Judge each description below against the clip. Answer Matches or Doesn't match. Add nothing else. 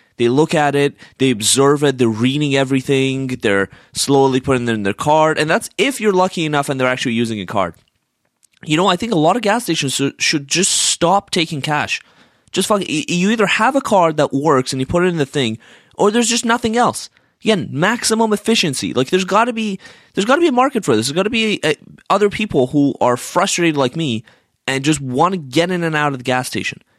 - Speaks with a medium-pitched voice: Matches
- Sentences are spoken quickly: Matches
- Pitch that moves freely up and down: Matches